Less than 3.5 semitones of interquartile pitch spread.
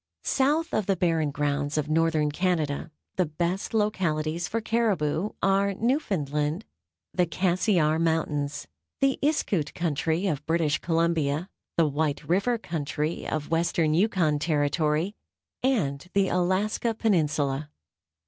No: average, 4.5 semitones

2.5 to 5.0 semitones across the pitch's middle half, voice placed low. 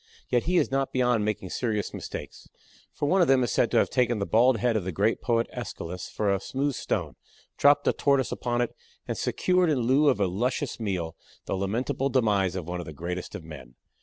No: wide, 5.6 semitones; low, 115 Hz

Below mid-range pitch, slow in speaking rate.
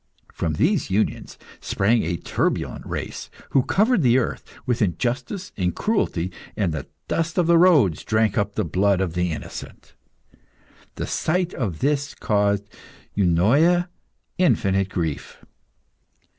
Yes: low, 110 Hz; slow, 130 wpm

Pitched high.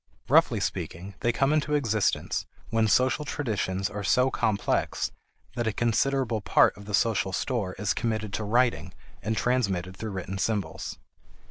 No: low, 110 Hz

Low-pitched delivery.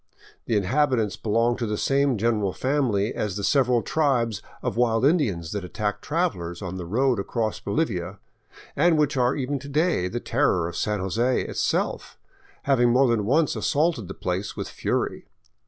Yes: low, 115 Hz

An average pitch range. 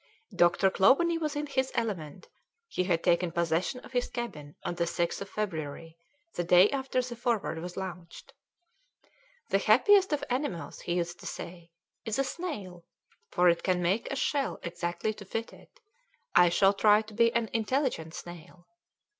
No: wide, 6.0 semitones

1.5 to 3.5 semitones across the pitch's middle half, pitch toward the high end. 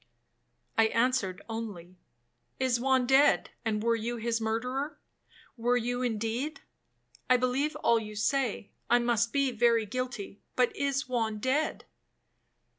Yes: narrow, 2.5 semitones; high, 240 Hz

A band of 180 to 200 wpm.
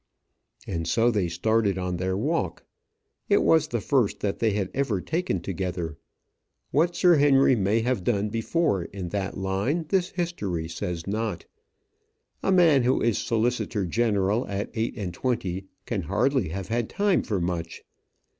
No: average, 155 wpm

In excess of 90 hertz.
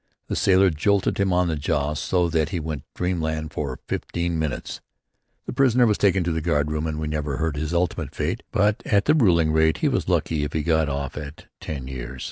No: very low, 80 Hz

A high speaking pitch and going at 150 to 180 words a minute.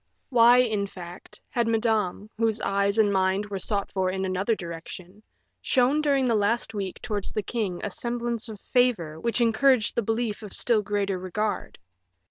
Yes: high, 210 Hz; average, 170 wpm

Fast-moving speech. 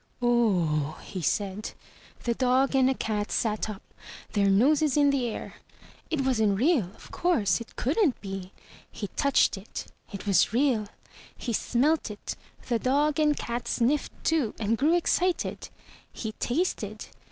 No: average, 155 wpm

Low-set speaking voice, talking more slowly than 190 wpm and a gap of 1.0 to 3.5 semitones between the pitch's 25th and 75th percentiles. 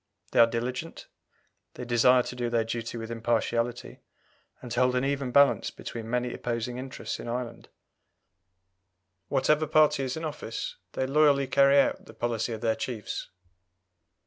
Yes: low, 125 Hz; average, 155 wpm; narrow, 2.6 semitones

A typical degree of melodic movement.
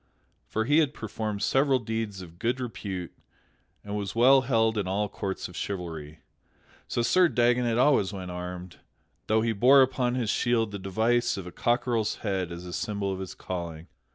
Yes: average, 4.5 semitones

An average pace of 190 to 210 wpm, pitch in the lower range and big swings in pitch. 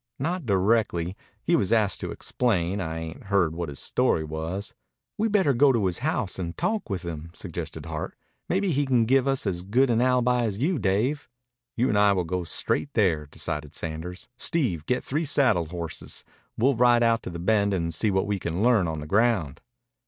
Yes: average, 195 wpm; low, 100 Hz; wide, 6.5 semitones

